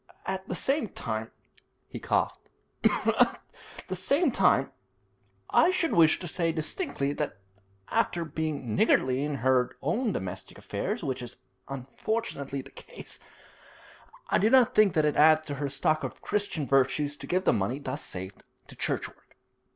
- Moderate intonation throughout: No, wide, 5.8 semitones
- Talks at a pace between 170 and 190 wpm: No, average, 150 wpm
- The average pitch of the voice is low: No, medium, 150 Hz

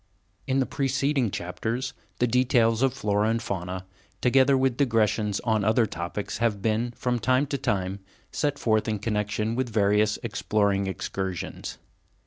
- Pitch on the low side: Yes, low, 110 Hz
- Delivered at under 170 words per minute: Yes, average, 150 wpm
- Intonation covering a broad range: No, average, 3.6 semitones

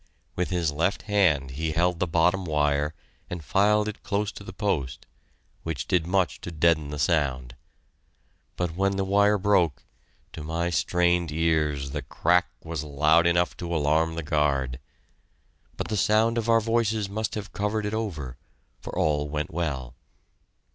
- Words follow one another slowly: No, average, 160 wpm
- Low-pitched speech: Yes, very low, 85 Hz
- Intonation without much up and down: No, average, 4.7 semitones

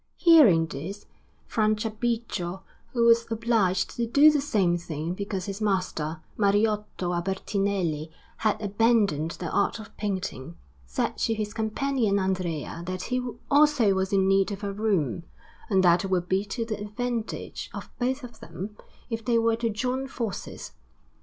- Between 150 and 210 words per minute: Yes, average, 155 wpm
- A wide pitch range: No, average, 3.7 semitones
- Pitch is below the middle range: No, high, 205 Hz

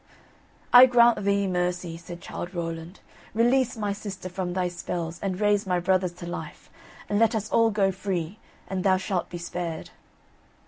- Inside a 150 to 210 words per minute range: Yes, average, 170 wpm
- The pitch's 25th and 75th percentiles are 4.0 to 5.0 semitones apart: No, average, 2.8 semitones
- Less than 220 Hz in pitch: Yes, medium, 185 Hz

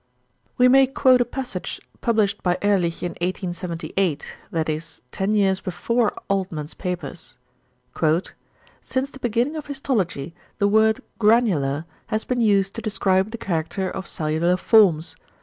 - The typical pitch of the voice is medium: No, high, 195 Hz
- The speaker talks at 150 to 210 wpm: No, slow, 135 wpm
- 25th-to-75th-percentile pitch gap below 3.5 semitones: No, average, 5.1 semitones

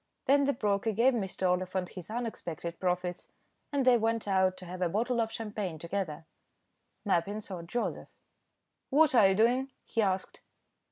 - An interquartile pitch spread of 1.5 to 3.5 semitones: No, average, 4.2 semitones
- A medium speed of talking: Yes, average, 160 wpm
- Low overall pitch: No, high, 200 Hz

